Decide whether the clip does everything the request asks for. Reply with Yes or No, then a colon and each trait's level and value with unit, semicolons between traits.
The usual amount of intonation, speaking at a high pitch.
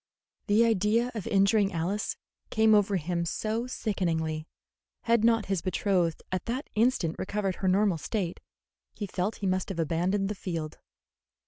Yes: average, 3.4 semitones; high, 195 Hz